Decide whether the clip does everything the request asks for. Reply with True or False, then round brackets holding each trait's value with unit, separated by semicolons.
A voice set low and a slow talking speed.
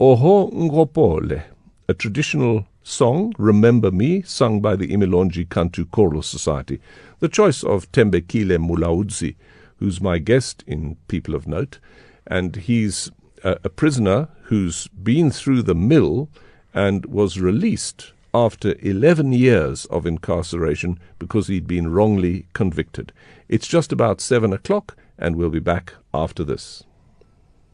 True (100 Hz; 130 wpm)